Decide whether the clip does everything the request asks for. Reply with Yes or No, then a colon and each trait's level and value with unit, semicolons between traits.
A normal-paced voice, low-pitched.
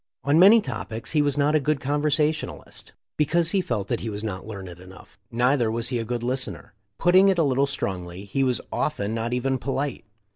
No: fast, 210 wpm; low, 130 Hz